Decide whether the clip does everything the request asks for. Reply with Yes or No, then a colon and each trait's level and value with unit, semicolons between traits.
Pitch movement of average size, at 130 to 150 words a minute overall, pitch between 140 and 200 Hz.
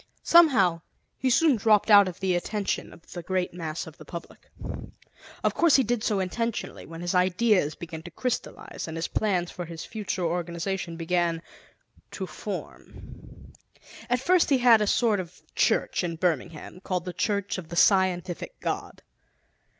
No: average, 4.0 semitones; average, 165 wpm; medium, 185 Hz